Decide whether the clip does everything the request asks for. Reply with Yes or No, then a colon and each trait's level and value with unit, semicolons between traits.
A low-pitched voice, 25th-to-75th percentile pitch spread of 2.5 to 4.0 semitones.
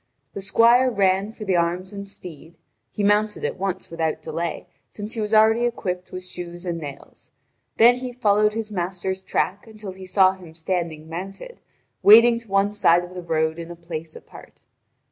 No: high, 190 Hz; average, 3.6 semitones